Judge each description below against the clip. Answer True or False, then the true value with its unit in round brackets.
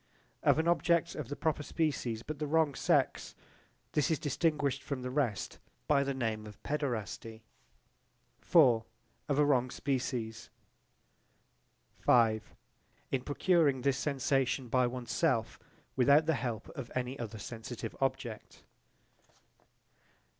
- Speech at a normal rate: False (120 wpm)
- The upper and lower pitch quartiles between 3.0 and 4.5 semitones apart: True (3.6 semitones)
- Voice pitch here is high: False (135 Hz)